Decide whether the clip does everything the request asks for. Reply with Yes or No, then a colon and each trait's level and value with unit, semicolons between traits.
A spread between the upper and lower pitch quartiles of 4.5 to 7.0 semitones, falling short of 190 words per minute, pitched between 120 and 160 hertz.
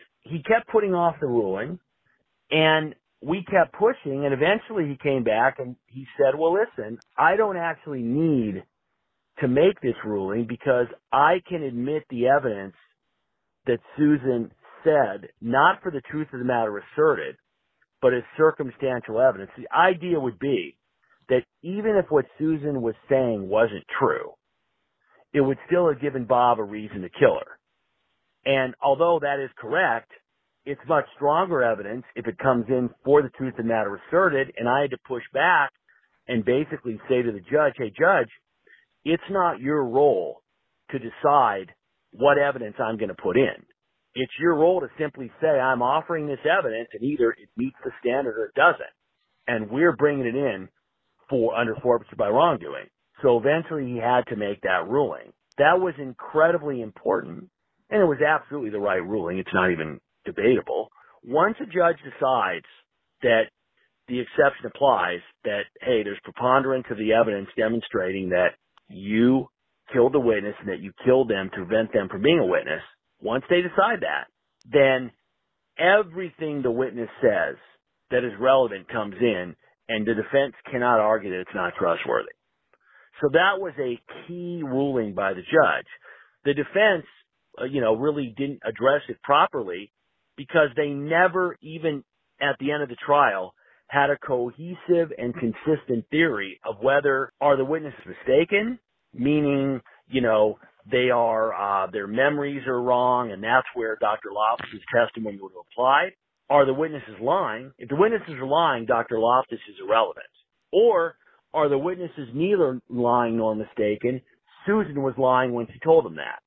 Yes: average, 4.9 semitones; average, 160 wpm; low, 135 Hz